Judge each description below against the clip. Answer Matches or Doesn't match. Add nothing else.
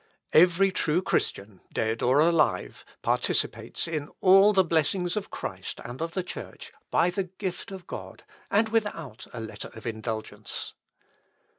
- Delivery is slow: Doesn't match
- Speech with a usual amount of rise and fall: Doesn't match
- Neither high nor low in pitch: Matches